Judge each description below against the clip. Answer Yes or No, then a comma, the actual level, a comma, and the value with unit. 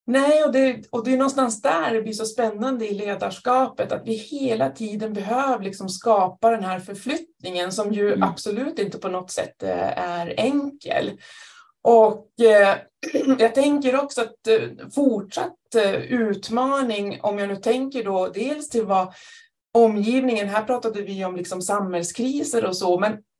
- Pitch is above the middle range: Yes, high, 225 Hz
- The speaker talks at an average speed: Yes, average, 150 wpm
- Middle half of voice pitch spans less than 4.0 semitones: No, average, 4.5 semitones